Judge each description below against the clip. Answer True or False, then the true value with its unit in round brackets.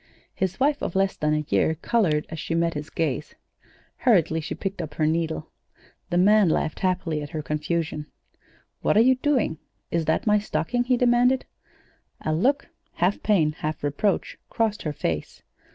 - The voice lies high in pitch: False (170 Hz)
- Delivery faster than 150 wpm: True (170 wpm)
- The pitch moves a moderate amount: False (5.7 semitones)